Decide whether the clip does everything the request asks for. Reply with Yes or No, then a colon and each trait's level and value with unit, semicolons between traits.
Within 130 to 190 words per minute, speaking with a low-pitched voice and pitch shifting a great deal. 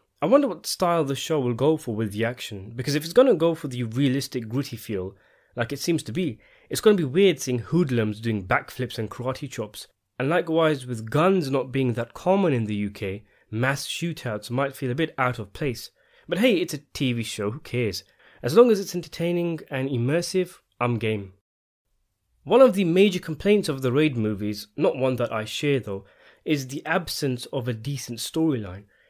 No: fast, 205 wpm; low, 130 Hz; wide, 6.1 semitones